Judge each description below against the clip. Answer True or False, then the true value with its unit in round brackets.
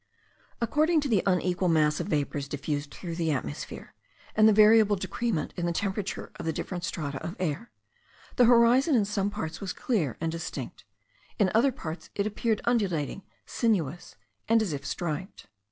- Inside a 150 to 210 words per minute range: True (170 wpm)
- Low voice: False (190 Hz)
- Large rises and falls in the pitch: True (5.7 semitones)